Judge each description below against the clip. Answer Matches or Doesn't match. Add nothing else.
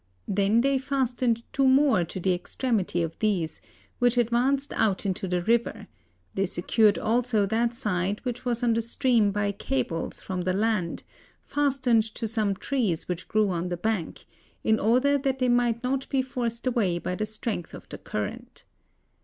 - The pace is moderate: Matches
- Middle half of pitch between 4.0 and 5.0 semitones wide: Matches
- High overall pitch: Matches